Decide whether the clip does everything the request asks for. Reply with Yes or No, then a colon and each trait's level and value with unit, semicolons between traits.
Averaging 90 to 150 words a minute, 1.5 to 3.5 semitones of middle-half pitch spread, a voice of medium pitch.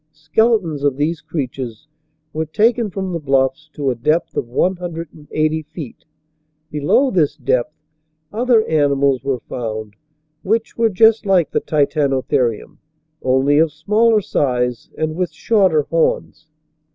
No: average, 145 wpm; average, 5.2 semitones; medium, 155 Hz